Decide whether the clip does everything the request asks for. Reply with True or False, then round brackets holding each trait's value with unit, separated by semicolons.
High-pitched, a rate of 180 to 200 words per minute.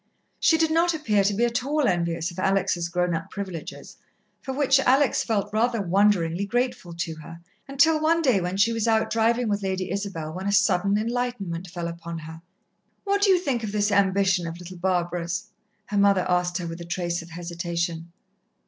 True (195 Hz; 195 wpm)